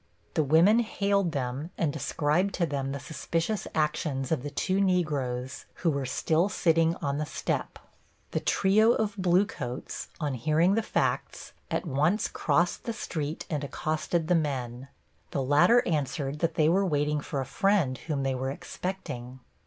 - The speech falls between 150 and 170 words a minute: Yes, average, 160 wpm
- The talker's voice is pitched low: No, medium, 155 Hz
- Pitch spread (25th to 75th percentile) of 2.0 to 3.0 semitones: No, average, 4.4 semitones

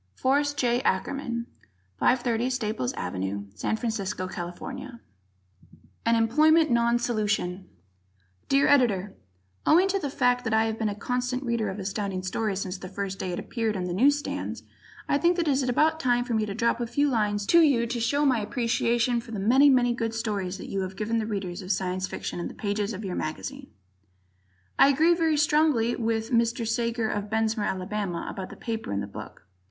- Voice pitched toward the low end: No, high, 230 Hz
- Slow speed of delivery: No, average, 195 wpm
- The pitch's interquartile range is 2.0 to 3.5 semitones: No, average, 3.9 semitones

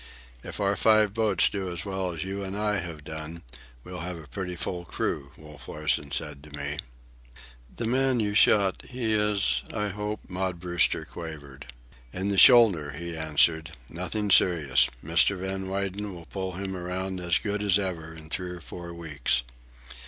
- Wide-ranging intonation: No, average, 3.8 semitones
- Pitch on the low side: Yes, very low, 90 Hz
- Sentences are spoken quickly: No, average, 165 wpm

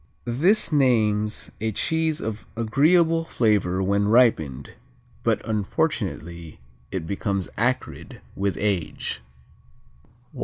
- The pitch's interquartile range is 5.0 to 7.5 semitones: Yes, average, 5.3 semitones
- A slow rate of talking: Yes, slow, 90 wpm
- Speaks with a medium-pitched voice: No, low, 110 Hz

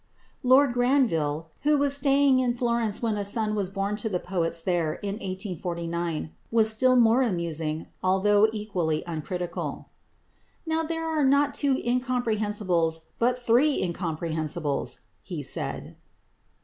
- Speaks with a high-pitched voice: Yes, high, 210 Hz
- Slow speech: Yes, slow, 130 wpm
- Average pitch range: No, wide, 6.7 semitones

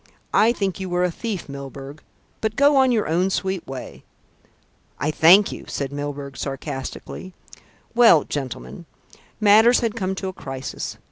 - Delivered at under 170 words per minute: Yes, average, 155 wpm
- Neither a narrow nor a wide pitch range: No, wide, 7.0 semitones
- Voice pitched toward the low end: No, medium, 180 Hz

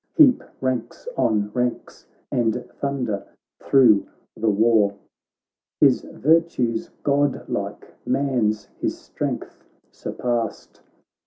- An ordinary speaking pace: No, slow, 85 wpm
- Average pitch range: Yes, average, 4.1 semitones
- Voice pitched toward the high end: No, low, 120 Hz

